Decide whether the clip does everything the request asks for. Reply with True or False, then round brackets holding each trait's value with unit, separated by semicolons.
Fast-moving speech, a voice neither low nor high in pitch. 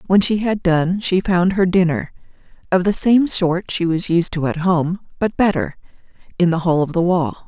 False (195 wpm; 180 Hz)